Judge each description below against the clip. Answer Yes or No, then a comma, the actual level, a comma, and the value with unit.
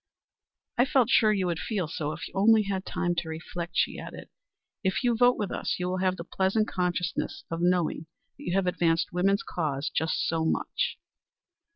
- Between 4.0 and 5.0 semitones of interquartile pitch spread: No, average, 2.9 semitones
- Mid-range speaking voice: Yes, medium, 180 Hz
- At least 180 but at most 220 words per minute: Yes, average, 195 wpm